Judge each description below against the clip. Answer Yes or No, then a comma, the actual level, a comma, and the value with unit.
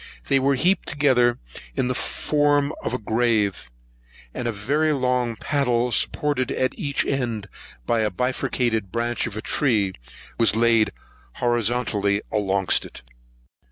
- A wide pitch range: No, average, 3.8 semitones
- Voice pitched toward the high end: No, low, 120 Hz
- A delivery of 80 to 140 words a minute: Yes, slow, 135 wpm